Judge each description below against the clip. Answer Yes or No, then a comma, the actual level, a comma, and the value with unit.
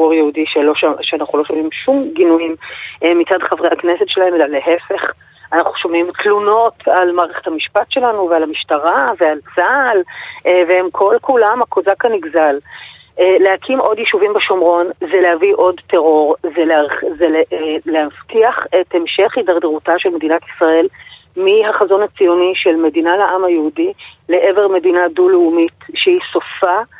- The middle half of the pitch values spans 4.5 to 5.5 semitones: Yes, average, 5.2 semitones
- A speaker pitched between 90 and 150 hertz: No, medium, 180 Hz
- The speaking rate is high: No, average, 125 wpm